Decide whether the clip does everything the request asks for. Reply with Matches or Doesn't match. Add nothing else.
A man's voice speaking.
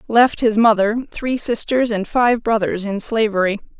Doesn't match